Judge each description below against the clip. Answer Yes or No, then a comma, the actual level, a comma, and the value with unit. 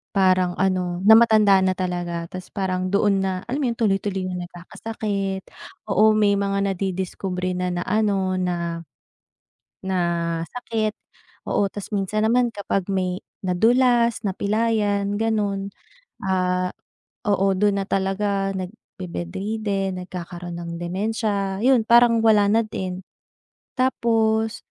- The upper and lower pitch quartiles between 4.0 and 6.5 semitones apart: No, average, 2.8 semitones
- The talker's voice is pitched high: Yes, high, 195 Hz